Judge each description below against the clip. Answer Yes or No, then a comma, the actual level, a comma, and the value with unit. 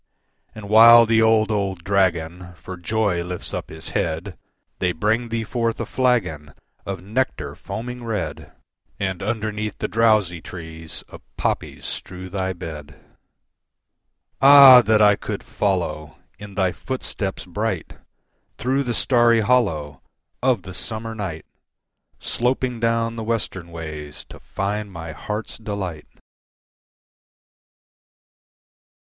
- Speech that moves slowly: Yes, slow, 120 wpm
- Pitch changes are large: No, average, 4.8 semitones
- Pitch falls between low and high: No, low, 100 Hz